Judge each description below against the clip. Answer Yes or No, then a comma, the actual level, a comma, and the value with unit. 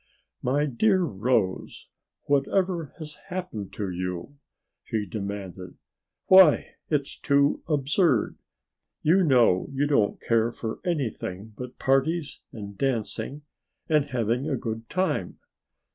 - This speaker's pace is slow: Yes, slow, 115 wpm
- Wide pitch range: Yes, wide, 5.7 semitones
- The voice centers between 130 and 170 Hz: Yes, low, 135 Hz